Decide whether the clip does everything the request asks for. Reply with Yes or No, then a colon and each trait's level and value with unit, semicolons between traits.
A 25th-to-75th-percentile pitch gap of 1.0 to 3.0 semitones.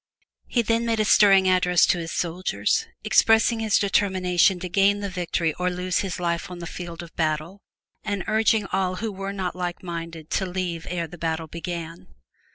Yes: average, 2.7 semitones